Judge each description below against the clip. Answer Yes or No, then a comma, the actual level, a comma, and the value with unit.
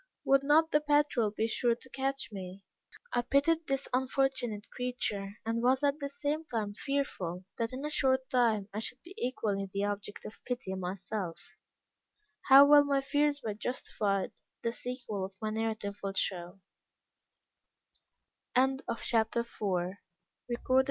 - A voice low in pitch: No, high, 240 Hz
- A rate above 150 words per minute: No, average, 140 wpm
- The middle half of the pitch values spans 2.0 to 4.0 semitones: No, average, 5.2 semitones